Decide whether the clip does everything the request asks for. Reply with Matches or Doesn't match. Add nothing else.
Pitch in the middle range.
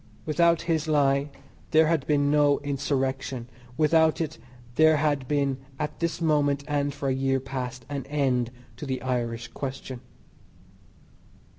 Matches